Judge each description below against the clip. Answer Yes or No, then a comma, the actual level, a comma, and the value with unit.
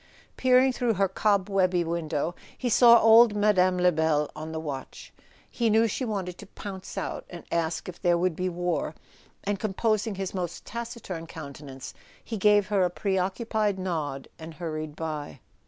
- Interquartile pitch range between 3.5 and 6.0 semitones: Yes, average, 4.4 semitones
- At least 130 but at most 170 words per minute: Yes, average, 165 wpm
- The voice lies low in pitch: No, medium, 185 Hz